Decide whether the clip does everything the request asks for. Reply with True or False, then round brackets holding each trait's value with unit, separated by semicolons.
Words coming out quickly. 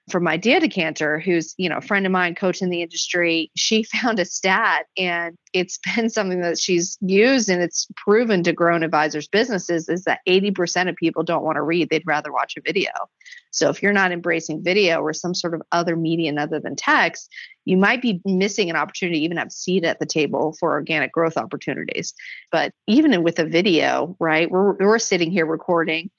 True (210 wpm)